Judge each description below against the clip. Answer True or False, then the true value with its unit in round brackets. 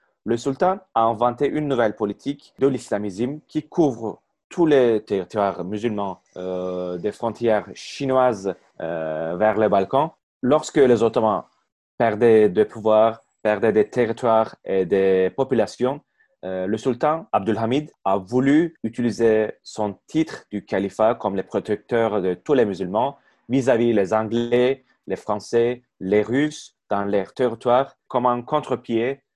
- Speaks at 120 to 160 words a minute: True (135 wpm)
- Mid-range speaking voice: False (115 Hz)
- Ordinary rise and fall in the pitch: True (3.6 semitones)